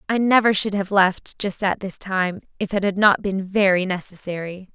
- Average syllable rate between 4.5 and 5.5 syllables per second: Yes, 4.8 syllables/s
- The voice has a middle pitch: No, high, 195 Hz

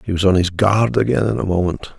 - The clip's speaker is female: No, male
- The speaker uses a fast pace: Yes, fast, 270 wpm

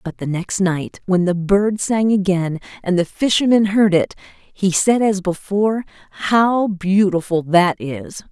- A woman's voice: Yes, female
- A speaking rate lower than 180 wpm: Yes, average, 160 wpm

